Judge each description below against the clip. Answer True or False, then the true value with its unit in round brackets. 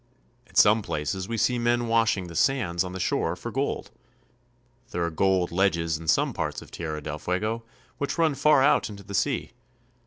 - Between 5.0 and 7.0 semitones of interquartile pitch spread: True (5.6 semitones)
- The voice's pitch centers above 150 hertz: False (100 Hz)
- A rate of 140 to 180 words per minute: False (190 wpm)